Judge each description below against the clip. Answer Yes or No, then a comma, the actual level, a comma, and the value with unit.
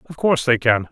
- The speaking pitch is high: No, low, 130 Hz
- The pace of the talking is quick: Yes, fast, 260 wpm